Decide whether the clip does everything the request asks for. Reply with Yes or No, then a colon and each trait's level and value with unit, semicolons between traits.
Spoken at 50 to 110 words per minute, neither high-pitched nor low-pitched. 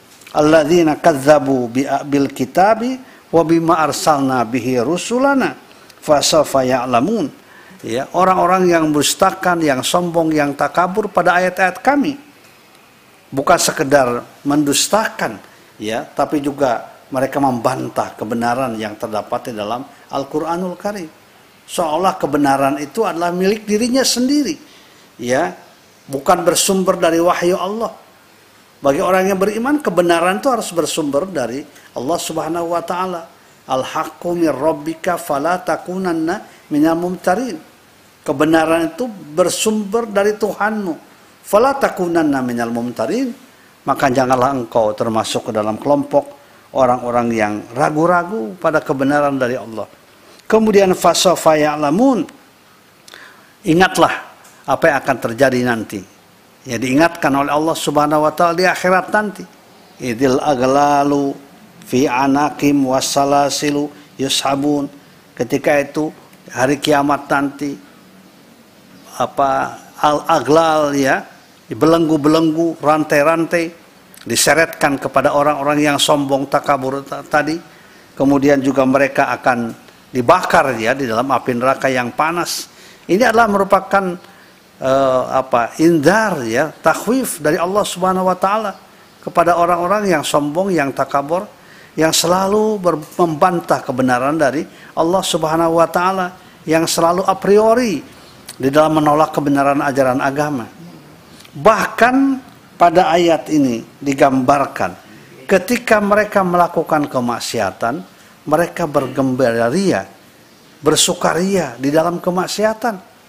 Yes: average, 105 wpm; medium, 165 Hz